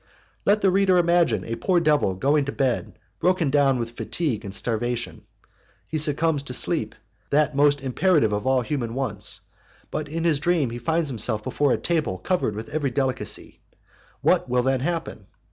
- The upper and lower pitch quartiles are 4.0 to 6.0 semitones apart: Yes, average, 5.1 semitones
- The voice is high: No, medium, 140 Hz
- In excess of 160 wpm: Yes, average, 175 wpm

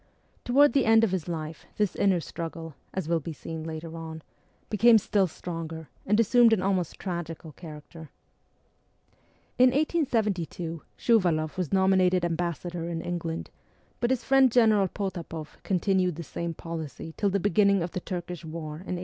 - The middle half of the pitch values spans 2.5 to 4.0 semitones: Yes, average, 3.7 semitones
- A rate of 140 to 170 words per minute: Yes, average, 160 wpm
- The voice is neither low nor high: Yes, medium, 175 Hz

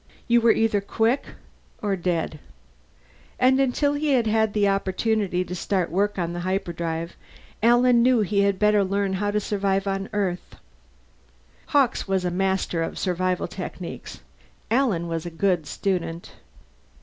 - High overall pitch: Yes, high, 195 Hz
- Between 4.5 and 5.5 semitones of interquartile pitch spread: No, average, 3.5 semitones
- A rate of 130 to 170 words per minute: Yes, average, 145 wpm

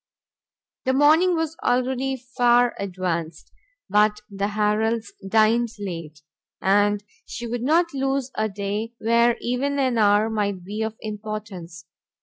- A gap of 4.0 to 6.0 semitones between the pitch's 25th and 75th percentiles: No, average, 3.4 semitones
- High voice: Yes, high, 220 Hz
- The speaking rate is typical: No, slow, 130 wpm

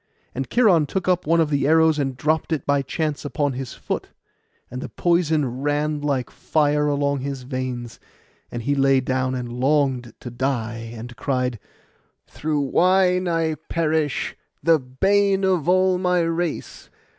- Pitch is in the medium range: Yes, medium, 145 Hz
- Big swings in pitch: No, average, 4.1 semitones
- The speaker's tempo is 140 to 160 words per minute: Yes, average, 155 wpm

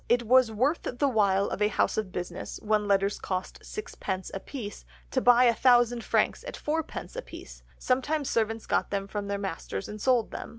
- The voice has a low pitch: No, high, 220 Hz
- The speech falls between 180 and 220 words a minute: Yes, average, 185 wpm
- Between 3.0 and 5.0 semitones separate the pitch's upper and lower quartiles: Yes, average, 4.0 semitones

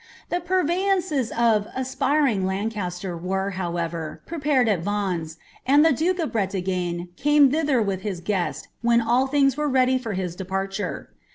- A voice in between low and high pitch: No, high, 220 Hz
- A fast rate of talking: No, average, 160 wpm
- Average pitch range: No, wide, 7.0 semitones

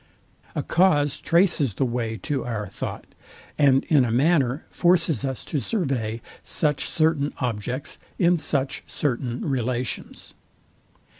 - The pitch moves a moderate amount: Yes, average, 4.4 semitones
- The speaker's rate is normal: No, slow, 125 wpm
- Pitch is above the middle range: No, low, 135 Hz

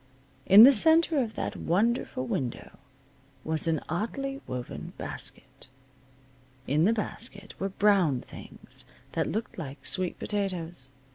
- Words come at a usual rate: No, slow, 125 wpm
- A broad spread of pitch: Yes, wide, 6.1 semitones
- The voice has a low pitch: No, high, 195 Hz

